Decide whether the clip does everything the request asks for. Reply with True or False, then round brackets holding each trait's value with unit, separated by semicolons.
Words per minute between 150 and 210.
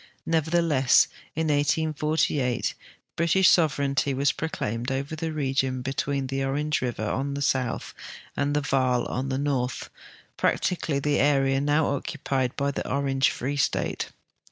False (135 wpm)